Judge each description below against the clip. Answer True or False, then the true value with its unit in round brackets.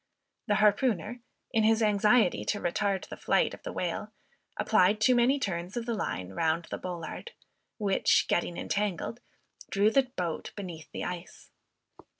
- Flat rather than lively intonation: False (4.2 semitones)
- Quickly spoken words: False (155 wpm)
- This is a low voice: False (205 Hz)